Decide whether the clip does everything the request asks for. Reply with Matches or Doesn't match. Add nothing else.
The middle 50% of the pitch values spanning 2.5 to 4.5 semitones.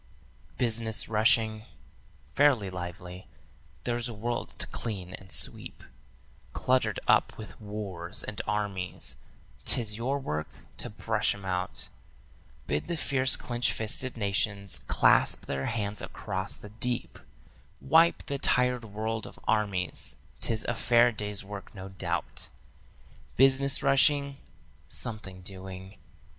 Matches